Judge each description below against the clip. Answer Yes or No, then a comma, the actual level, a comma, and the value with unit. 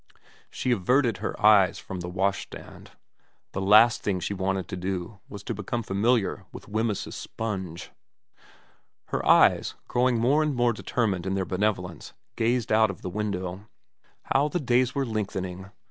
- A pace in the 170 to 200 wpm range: No, average, 155 wpm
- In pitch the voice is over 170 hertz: No, low, 105 Hz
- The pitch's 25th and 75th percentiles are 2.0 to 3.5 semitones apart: No, average, 4.0 semitones